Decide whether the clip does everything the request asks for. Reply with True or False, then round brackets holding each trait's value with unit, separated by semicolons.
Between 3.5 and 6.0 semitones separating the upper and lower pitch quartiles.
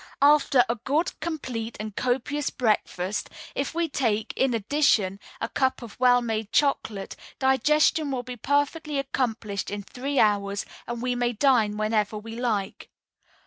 True (4.5 semitones)